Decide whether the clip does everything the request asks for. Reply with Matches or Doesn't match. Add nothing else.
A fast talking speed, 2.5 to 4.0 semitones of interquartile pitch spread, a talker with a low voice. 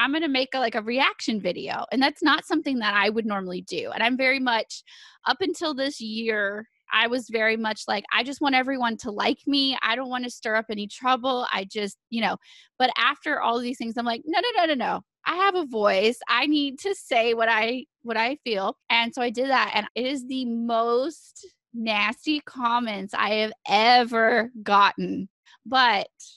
Doesn't match